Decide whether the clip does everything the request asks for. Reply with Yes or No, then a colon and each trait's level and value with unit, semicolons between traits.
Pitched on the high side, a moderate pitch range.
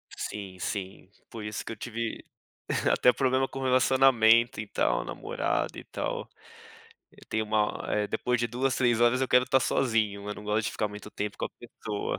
No: low, 110 Hz; average, 3.2 semitones